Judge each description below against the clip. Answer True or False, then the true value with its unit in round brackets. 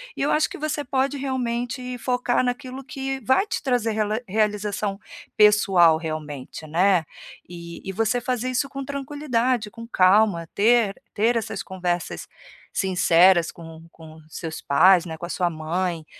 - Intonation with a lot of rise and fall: True (6.3 semitones)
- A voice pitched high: True (210 Hz)